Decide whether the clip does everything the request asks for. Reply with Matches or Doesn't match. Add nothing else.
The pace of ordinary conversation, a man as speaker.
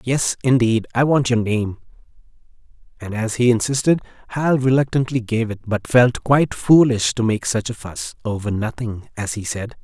Matches